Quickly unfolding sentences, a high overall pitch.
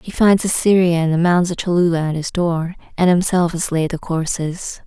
No: fast, 210 wpm; medium, 175 Hz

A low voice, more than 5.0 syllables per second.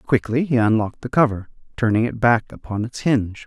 Yes: low, 115 Hz; 5.8 syllables/s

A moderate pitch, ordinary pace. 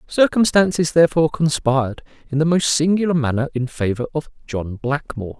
Yes: medium, 145 Hz; average, 145 wpm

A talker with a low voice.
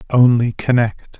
Yes: low, 120 Hz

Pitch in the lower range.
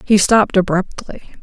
No: high, 200 Hz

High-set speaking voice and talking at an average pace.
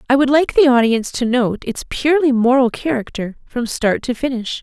Yes: very high, 255 Hz; average, 195 wpm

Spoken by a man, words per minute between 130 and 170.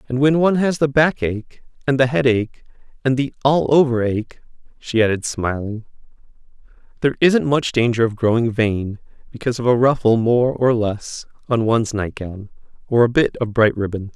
No: male; average, 180 wpm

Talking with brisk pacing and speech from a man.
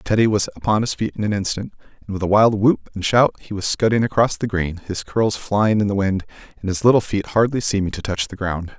Yes: fast, 255 wpm; male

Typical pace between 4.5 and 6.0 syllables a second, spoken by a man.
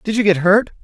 No: 6.3 syllables/s; male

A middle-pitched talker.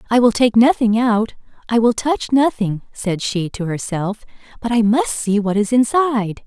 No: high, 225 Hz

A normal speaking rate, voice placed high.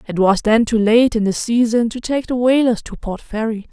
No: fast, 240 wpm; high, 230 Hz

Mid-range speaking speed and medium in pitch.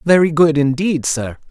Yes: average, 160 wpm; medium, 155 Hz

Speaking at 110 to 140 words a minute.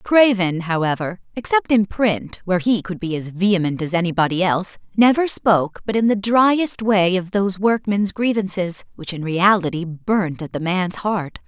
No: average, 175 wpm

